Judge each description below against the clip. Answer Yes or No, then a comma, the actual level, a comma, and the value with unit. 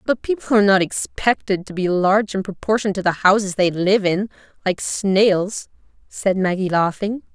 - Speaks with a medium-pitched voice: No, high, 195 Hz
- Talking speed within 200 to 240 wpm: No, average, 170 wpm